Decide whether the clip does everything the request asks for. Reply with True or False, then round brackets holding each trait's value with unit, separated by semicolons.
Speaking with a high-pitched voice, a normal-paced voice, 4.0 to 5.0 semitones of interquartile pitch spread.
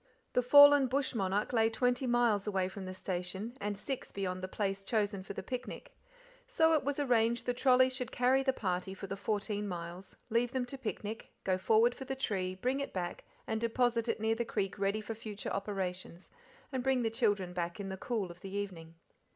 False (215 Hz; 210 wpm; 4.3 semitones)